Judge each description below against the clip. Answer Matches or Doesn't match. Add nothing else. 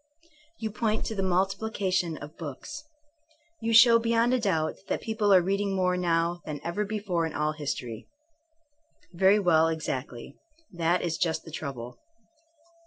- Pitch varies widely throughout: Doesn't match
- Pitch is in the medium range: Matches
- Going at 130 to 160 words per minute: Matches